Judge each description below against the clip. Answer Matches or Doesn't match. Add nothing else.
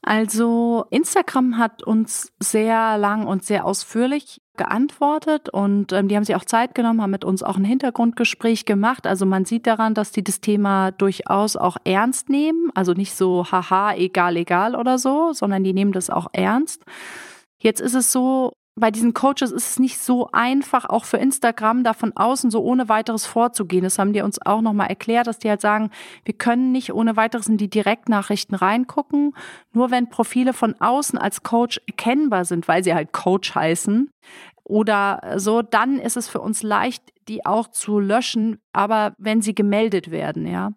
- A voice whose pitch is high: Matches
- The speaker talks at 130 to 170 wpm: Doesn't match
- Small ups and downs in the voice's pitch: Doesn't match